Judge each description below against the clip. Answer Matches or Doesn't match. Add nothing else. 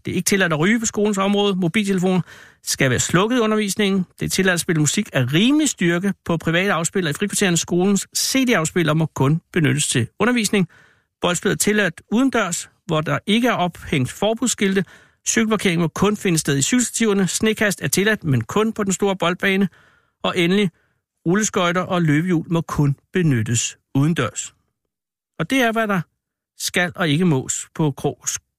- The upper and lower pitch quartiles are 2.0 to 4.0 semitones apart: Doesn't match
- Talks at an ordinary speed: Matches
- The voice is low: Doesn't match